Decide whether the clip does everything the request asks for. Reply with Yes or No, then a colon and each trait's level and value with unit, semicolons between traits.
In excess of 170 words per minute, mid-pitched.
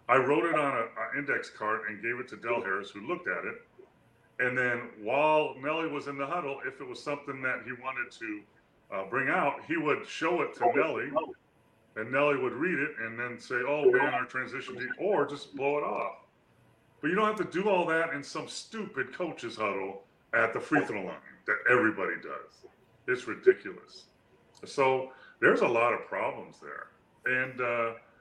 Yes: average, 195 wpm; medium, 160 Hz